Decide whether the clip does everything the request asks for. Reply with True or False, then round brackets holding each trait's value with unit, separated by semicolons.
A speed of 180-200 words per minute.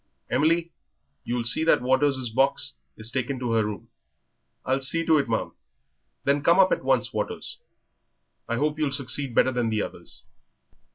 False (165 wpm)